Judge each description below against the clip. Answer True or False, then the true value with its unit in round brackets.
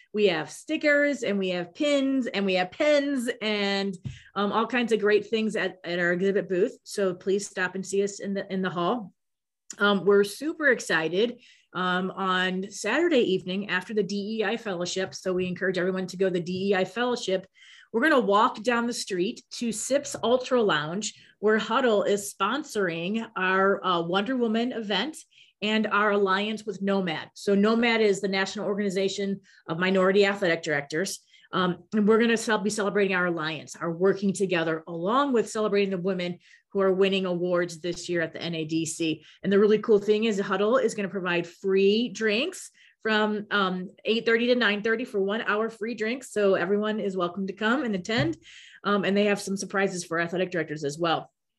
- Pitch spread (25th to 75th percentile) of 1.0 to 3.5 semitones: True (3.0 semitones)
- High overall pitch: True (200 Hz)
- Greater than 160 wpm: True (185 wpm)